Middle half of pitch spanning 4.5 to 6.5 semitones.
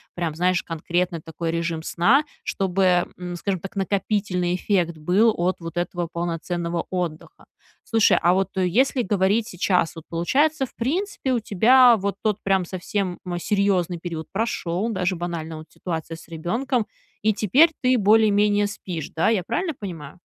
No: average, 3.8 semitones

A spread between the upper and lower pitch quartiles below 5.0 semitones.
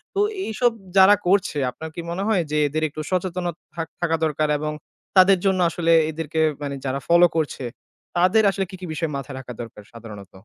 Yes: average, 3.8 semitones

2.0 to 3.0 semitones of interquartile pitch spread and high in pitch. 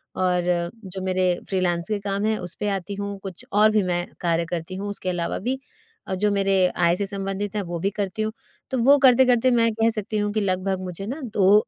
Yes: narrow, 2.6 semitones; high, 195 Hz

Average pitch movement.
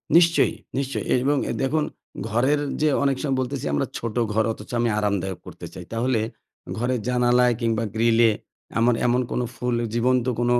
No: narrow, 2.3 semitones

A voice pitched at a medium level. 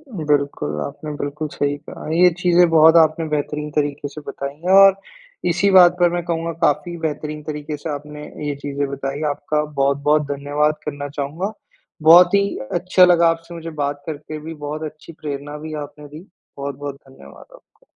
Yes: medium, 150 Hz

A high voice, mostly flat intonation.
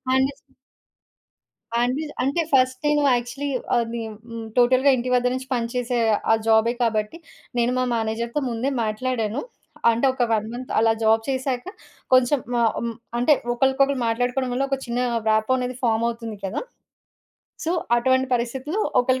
Yes: high, 245 Hz; narrow, 2.2 semitones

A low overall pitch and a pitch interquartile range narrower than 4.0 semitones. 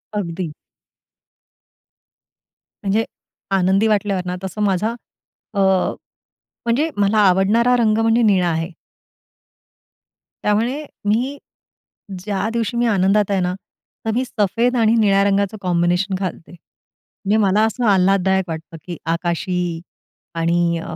No: high, 195 Hz; average, 3.2 semitones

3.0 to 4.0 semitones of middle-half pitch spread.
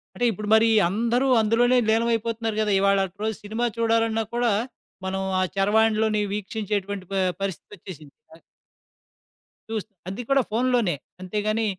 No: narrow, 2.4 semitones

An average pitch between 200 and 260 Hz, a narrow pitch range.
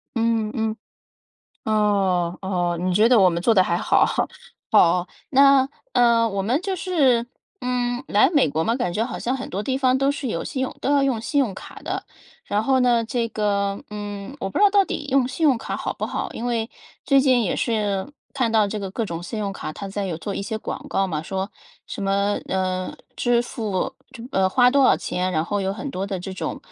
No: high, 220 Hz; average, 4.7 semitones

